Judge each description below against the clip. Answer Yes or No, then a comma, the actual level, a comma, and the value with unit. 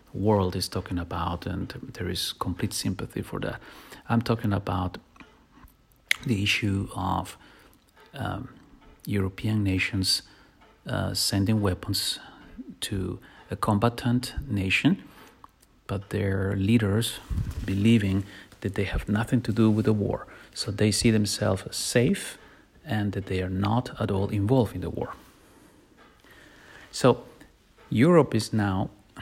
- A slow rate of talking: Yes, slow, 125 wpm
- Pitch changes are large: No, narrow, 2.5 semitones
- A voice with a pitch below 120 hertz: Yes, low, 100 Hz